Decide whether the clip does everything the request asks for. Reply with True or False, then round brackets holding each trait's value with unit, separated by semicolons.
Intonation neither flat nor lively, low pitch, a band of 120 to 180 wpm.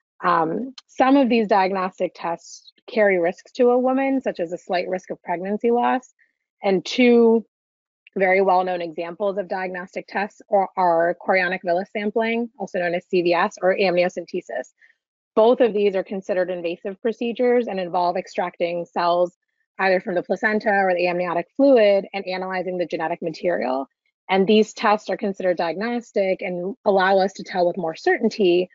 False (3.7 semitones; 190 Hz; 160 wpm)